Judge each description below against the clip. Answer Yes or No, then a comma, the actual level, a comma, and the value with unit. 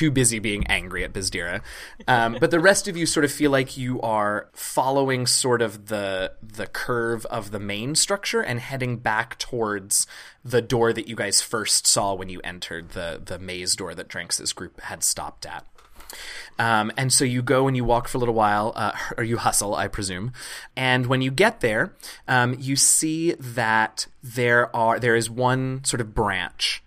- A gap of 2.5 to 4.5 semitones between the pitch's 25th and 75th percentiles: Yes, average, 3.8 semitones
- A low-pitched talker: Yes, low, 120 Hz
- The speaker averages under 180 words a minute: No, average, 195 wpm